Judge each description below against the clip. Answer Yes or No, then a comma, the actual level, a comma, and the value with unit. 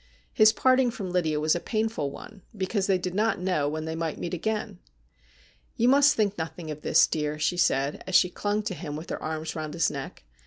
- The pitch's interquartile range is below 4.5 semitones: No, average, 5.3 semitones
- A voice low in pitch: No, medium, 175 Hz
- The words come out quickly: Yes, fast, 225 wpm